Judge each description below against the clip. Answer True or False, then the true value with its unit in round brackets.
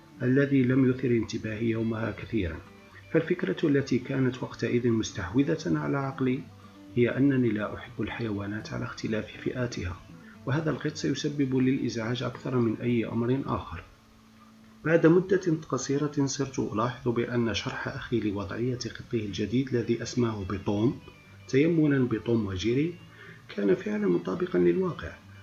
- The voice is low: True (120 Hz)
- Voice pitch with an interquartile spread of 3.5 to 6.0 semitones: True (4.1 semitones)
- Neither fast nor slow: True (120 wpm)